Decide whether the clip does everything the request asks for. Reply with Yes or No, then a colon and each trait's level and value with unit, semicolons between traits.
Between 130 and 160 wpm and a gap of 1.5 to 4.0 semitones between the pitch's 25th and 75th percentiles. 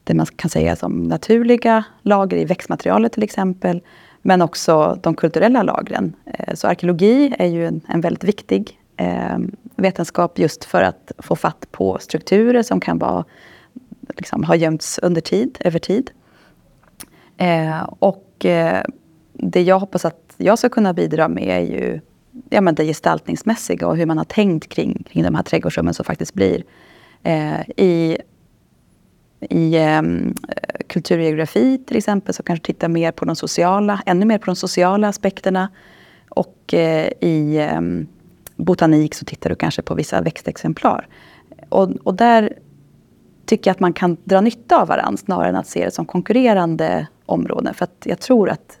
No: average, 150 wpm; average, 4.6 semitones